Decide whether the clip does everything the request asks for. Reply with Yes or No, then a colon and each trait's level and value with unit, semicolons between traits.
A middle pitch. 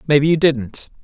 Yes: medium, 145 Hz